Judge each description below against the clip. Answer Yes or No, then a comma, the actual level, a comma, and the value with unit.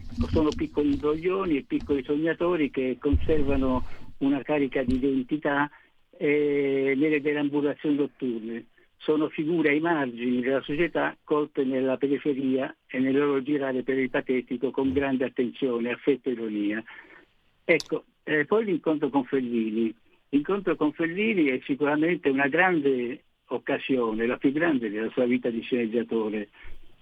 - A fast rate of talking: No, average, 135 wpm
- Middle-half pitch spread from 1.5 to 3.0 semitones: Yes, average, 2.7 semitones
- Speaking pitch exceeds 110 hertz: Yes, medium, 140 Hz